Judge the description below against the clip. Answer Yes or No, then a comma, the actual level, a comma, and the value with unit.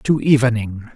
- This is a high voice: No, low, 120 Hz